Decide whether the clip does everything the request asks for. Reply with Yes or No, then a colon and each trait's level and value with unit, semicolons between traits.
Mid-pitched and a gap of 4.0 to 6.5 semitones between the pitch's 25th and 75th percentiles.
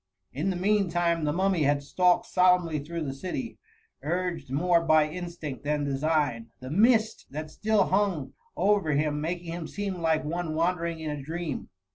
No: medium, 165 Hz; average, 3.2 semitones